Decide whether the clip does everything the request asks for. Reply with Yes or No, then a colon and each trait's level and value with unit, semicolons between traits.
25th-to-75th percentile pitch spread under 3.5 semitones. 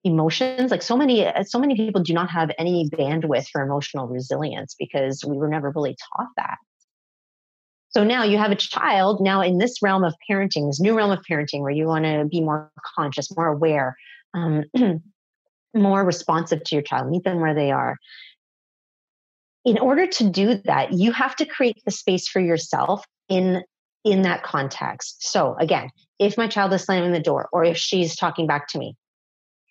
No: average, 5.0 semitones